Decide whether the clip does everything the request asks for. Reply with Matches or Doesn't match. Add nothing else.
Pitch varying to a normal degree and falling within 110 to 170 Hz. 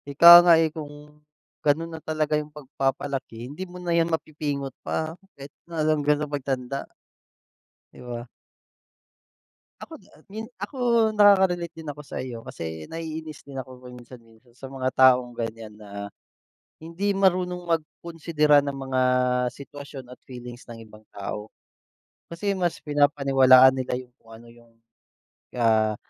Matches